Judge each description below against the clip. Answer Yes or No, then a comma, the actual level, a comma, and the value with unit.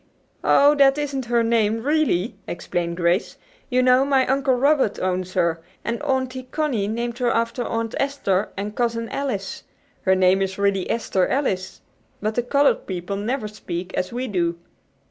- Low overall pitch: No, high, 230 Hz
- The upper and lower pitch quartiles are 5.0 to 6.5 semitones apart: Yes, wide, 5.6 semitones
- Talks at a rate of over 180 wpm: No, average, 165 wpm